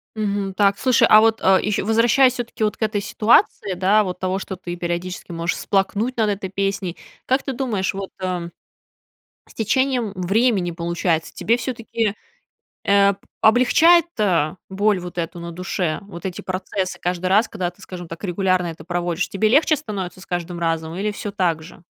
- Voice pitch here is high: Yes, high, 195 Hz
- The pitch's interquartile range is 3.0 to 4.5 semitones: Yes, average, 3.5 semitones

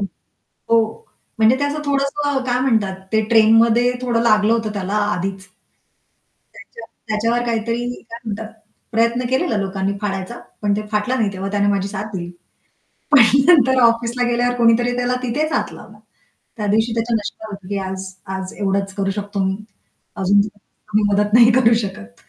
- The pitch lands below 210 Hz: No, high, 220 Hz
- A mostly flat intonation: No, average, 3.2 semitones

